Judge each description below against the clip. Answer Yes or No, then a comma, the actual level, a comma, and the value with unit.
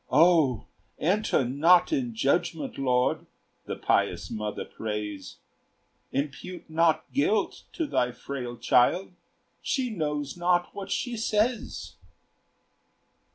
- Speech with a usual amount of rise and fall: No, wide, 8.2 semitones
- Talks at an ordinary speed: No, slow, 105 wpm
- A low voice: No, medium, 165 Hz